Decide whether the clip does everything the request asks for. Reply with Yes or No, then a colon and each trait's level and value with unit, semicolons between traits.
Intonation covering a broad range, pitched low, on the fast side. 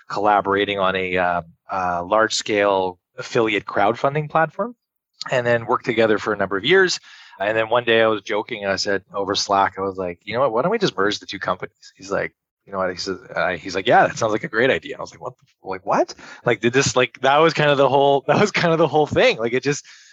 Yes: wide, 6.0 semitones; low, 115 Hz; fast, 260 wpm